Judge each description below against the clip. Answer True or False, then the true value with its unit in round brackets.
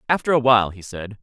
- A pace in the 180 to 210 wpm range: False (245 wpm)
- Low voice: True (115 Hz)